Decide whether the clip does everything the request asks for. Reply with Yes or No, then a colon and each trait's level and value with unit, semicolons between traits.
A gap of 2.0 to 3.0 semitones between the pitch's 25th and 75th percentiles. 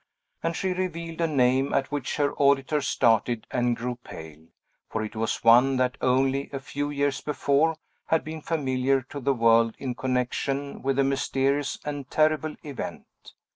Yes: narrow, 2.6 semitones